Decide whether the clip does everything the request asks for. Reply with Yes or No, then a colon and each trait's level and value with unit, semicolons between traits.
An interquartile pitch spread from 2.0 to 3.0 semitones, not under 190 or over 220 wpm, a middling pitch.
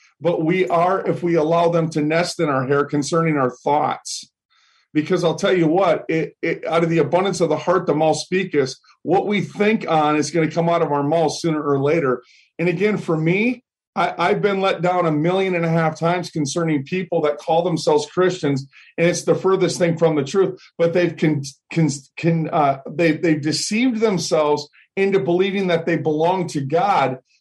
Yes: average, 2.7 semitones; fast, 205 wpm; medium, 165 Hz